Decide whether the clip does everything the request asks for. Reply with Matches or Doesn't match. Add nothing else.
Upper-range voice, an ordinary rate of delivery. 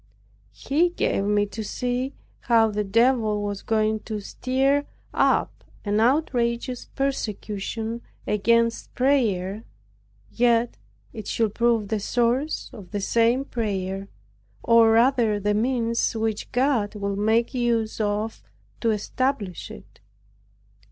Doesn't match